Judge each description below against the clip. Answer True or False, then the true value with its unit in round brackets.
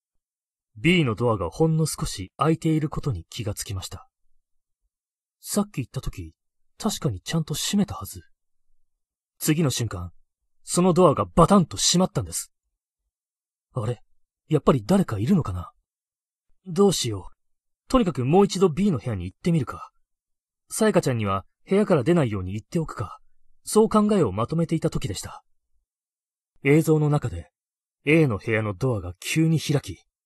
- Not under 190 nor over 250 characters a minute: False (310 characters per minute)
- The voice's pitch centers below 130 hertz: False (140 Hz)